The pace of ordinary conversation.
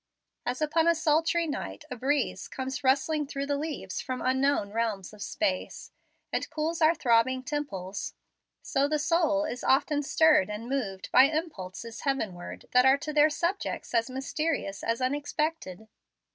Yes: average, 155 wpm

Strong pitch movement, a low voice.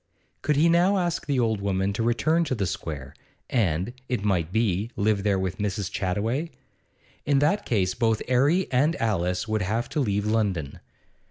Yes: wide, 5.7 semitones; low, 110 Hz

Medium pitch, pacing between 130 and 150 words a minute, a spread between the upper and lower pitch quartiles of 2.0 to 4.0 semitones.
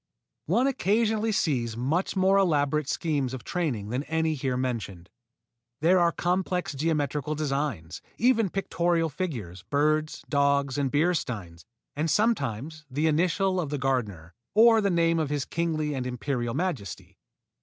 No: medium, 150 Hz; average, 145 wpm; average, 5.3 semitones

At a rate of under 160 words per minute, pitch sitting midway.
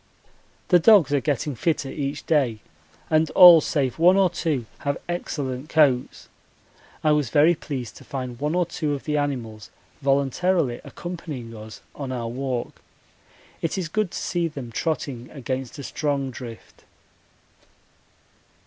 Yes: average, 145 wpm; medium, 145 Hz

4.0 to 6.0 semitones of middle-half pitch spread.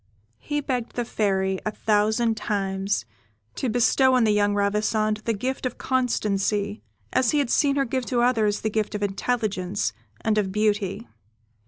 No: average, 3.1 semitones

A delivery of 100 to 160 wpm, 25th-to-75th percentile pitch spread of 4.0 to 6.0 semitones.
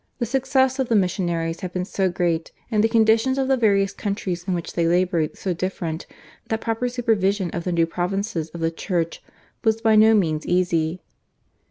No: average, 190 wpm; average, 4.6 semitones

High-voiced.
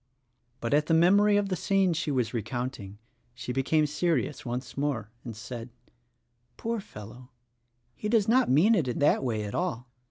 No: medium, 140 Hz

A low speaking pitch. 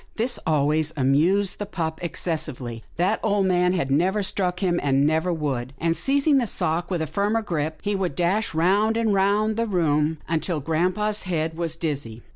No: medium, 175 Hz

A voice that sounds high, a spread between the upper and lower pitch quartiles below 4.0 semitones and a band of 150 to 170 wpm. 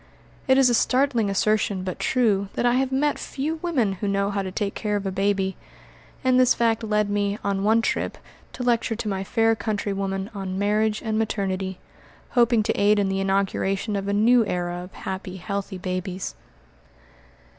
No: high, 205 Hz; average, 2.8 semitones; average, 185 wpm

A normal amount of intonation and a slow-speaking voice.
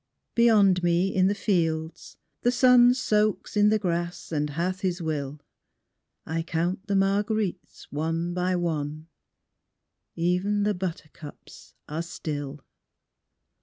Yes: average, 3.8 semitones; slow, 120 wpm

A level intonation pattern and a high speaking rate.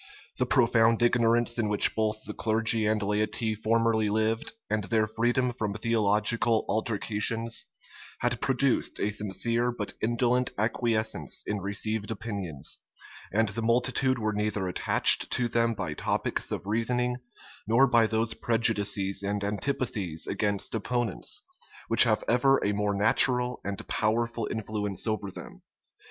No: narrow, 2.2 semitones; slow, 135 wpm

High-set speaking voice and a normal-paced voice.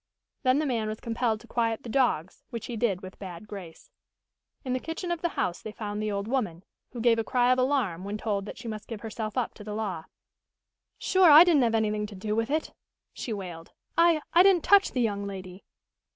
No: high, 225 Hz; fast, 225 wpm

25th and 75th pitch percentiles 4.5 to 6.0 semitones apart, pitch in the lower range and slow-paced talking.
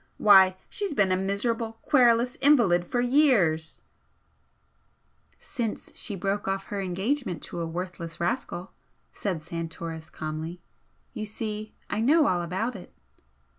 No: average, 5.1 semitones; high, 195 Hz; slow, 130 wpm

